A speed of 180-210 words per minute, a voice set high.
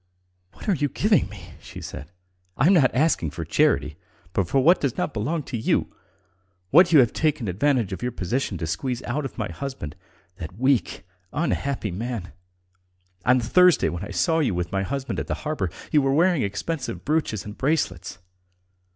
No: average, 185 wpm; low, 130 Hz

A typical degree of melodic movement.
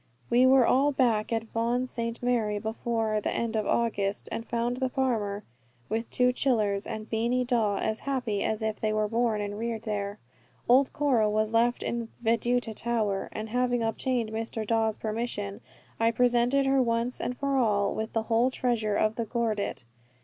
No: narrow, 2.2 semitones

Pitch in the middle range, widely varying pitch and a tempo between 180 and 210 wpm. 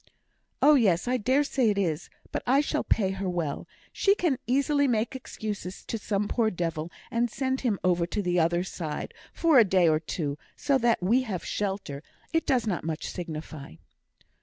No: high, 205 Hz; wide, 6.7 semitones; average, 190 wpm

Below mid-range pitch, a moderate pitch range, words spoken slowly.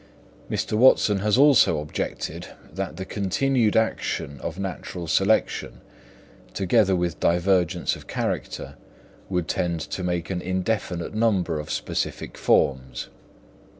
Yes: very low, 95 Hz; average, 3.7 semitones; slow, 115 wpm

